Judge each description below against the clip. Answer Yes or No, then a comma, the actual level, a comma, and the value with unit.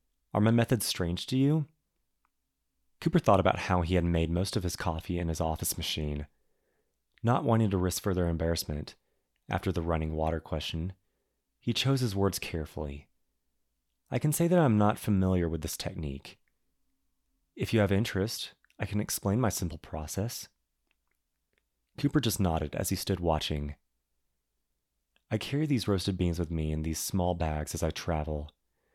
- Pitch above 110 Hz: No, very low, 90 Hz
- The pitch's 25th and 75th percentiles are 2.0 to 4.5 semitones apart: No, average, 5.2 semitones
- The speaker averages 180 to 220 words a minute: No, average, 165 wpm